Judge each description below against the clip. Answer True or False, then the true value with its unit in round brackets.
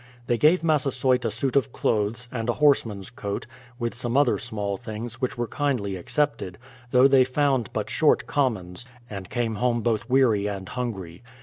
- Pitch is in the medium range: False (120 Hz)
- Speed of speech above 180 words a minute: False (175 wpm)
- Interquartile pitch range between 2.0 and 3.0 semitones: False (3.8 semitones)